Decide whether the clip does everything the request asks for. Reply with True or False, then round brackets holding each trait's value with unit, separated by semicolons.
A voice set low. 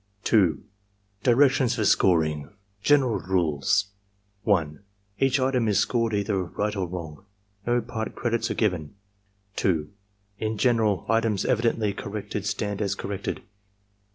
True (105 Hz)